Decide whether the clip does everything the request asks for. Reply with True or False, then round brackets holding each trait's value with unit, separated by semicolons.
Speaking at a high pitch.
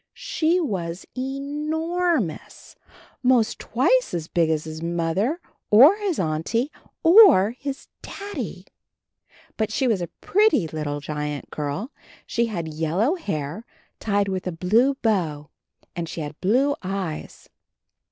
True (205 Hz)